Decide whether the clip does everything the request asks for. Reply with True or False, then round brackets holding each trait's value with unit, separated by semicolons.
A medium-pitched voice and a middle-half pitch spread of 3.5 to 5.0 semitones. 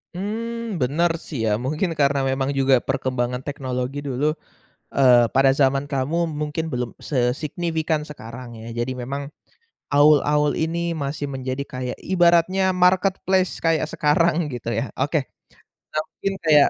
True (145 Hz; 4.1 semitones)